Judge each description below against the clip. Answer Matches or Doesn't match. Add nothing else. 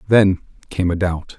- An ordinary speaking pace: Matches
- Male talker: Matches